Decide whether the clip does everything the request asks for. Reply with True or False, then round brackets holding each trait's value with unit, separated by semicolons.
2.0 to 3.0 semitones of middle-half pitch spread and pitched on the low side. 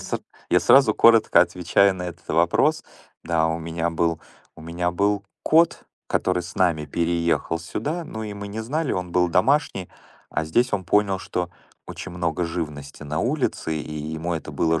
False (3.7 semitones; 90 Hz)